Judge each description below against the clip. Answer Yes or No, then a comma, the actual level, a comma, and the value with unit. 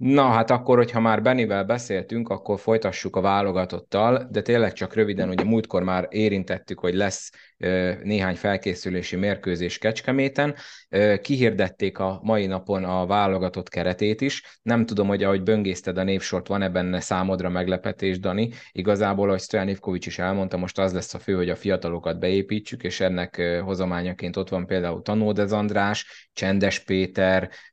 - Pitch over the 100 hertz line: No, very low, 95 Hz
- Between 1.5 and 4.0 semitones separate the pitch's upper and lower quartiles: Yes, narrow, 2.6 semitones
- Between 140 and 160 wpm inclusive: Yes, average, 150 wpm